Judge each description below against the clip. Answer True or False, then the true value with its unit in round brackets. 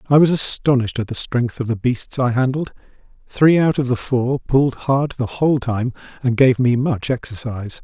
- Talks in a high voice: False (125 Hz)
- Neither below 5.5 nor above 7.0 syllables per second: False (5.1 syllables/s)